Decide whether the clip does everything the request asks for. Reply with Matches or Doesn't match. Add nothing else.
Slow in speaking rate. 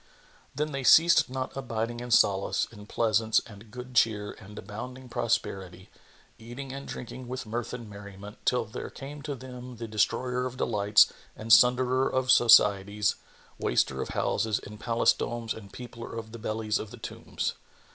Doesn't match